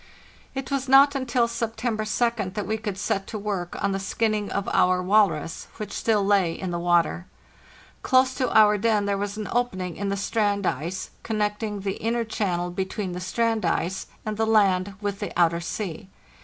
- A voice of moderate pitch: No, high, 205 Hz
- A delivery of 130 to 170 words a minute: No, average, 185 wpm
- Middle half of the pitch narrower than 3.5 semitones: Yes, average, 3.0 semitones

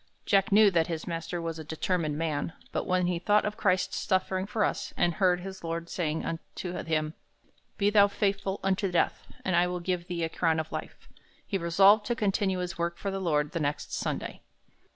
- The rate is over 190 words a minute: Yes, fast, 205 wpm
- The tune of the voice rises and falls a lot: No, average, 2.7 semitones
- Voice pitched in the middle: Yes, medium, 180 Hz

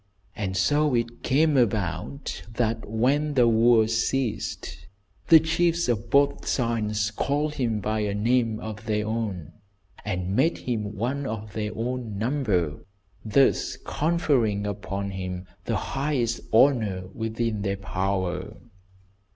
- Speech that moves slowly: Yes, slow, 125 wpm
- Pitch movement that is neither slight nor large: Yes, average, 4.0 semitones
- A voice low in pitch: Yes, low, 110 Hz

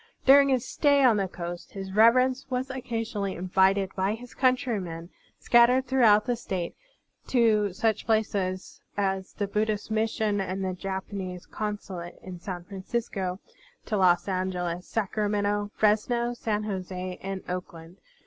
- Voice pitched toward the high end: Yes, high, 205 Hz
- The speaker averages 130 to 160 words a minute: Yes, average, 145 wpm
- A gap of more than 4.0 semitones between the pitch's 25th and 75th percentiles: No, average, 3.5 semitones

